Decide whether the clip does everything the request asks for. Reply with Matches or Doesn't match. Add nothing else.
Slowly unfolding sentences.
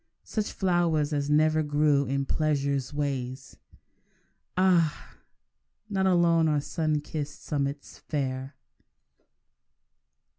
Matches